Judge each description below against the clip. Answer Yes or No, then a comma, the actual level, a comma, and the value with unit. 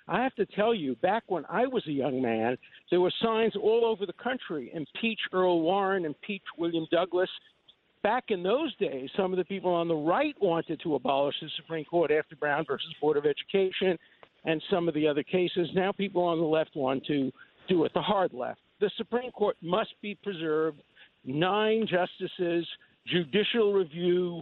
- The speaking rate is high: No, average, 185 wpm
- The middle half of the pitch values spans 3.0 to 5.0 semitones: Yes, average, 4.1 semitones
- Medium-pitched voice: Yes, medium, 180 Hz